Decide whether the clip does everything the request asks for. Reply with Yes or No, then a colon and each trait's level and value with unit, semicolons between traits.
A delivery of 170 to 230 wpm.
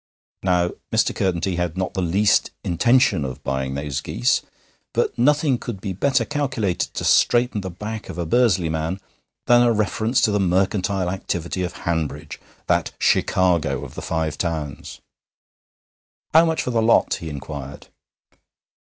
No: average, 155 wpm